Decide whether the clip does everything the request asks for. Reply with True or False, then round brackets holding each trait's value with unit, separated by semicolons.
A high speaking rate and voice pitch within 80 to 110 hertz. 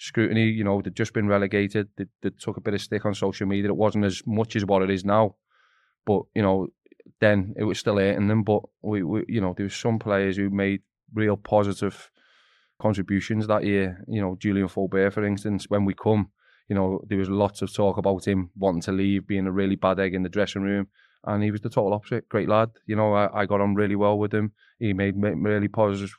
True (235 wpm; 100 Hz)